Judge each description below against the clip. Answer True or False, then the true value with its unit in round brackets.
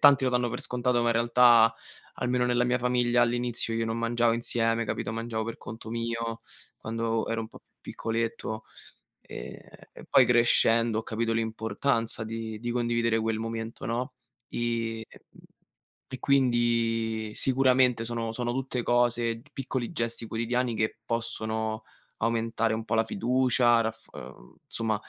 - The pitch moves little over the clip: True (1.3 semitones)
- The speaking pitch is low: True (115 Hz)